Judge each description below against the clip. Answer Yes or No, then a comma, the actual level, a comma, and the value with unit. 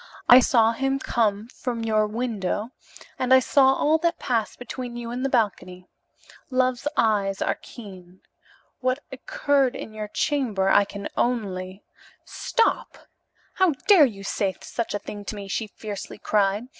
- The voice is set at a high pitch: Yes, high, 230 Hz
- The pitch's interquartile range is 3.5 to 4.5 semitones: Yes, average, 4.0 semitones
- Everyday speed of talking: Yes, average, 155 wpm